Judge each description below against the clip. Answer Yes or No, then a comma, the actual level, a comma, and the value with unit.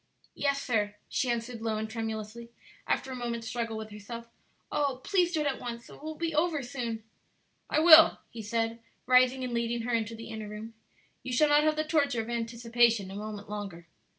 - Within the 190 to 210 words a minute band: Yes, fast, 205 wpm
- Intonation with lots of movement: No, average, 3.3 semitones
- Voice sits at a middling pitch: No, high, 235 Hz